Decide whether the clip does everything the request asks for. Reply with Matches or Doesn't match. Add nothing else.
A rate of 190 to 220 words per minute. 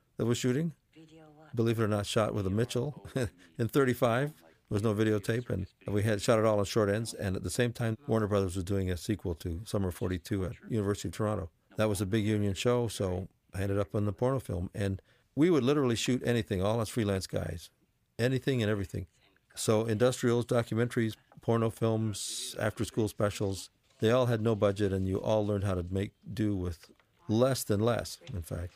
Matches